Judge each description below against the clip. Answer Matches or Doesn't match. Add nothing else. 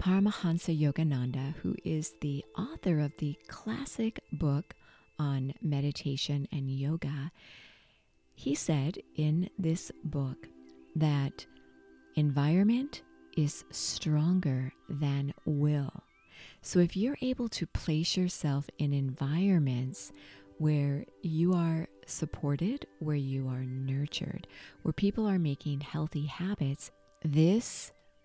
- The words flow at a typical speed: Doesn't match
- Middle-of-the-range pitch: Matches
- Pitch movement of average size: Matches